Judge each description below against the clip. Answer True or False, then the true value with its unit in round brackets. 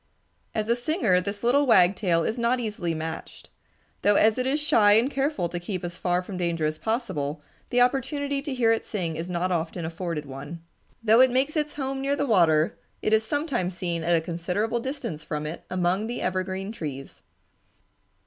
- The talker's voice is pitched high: True (200 Hz)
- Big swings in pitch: True (6.3 semitones)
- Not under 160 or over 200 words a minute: True (190 wpm)